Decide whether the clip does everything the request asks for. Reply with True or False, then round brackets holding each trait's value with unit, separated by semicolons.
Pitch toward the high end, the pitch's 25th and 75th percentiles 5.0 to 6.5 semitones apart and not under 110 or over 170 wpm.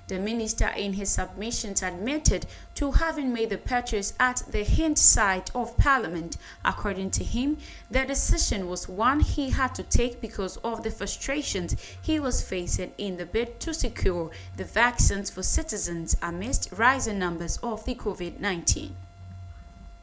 True (205 Hz; 5.4 semitones; 155 wpm)